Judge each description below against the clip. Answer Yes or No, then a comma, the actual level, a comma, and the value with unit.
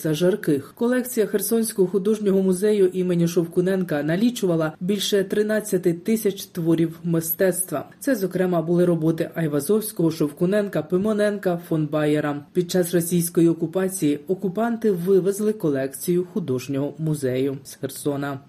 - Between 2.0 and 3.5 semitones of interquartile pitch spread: No, average, 3.9 semitones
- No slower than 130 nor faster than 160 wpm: No, average, 110 wpm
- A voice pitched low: No, medium, 180 Hz